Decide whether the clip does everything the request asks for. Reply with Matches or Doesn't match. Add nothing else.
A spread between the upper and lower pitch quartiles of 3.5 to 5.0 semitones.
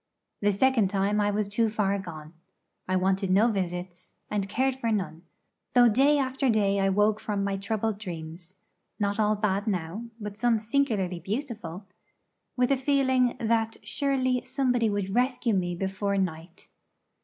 Matches